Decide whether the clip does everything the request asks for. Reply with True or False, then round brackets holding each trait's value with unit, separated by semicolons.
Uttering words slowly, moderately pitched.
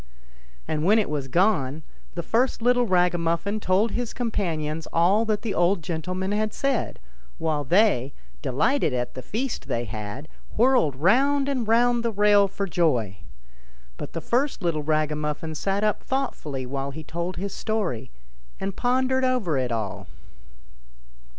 False (155 wpm; 180 Hz)